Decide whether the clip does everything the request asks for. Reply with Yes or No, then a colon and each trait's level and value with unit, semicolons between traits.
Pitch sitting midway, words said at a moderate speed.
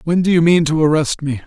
No: medium, 160 Hz; fast, 285 wpm